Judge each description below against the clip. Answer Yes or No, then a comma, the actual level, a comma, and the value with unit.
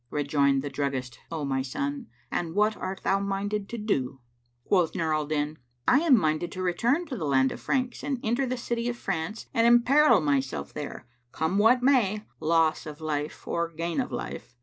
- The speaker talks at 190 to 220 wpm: Yes, average, 195 wpm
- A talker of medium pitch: Yes, medium, 175 Hz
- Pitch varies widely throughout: Yes, wide, 8.0 semitones